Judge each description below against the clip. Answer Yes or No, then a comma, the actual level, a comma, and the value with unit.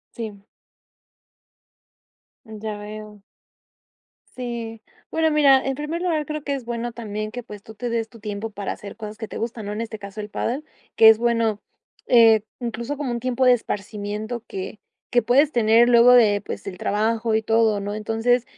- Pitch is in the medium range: No, high, 225 Hz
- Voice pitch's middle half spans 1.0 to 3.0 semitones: Yes, narrow, 2.4 semitones